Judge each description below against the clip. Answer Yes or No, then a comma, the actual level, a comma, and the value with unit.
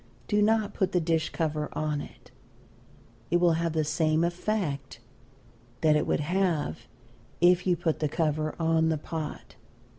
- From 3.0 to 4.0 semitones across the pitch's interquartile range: No, narrow, 2.4 semitones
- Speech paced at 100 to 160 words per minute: Yes, average, 150 wpm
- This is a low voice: No, medium, 160 Hz